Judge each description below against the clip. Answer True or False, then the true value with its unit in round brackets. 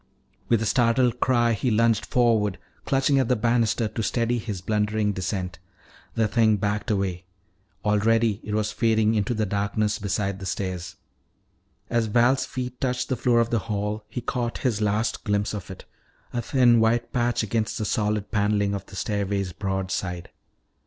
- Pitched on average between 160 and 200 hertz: False (110 Hz)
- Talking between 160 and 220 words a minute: True (170 wpm)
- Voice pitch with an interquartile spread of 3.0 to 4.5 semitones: False (2.5 semitones)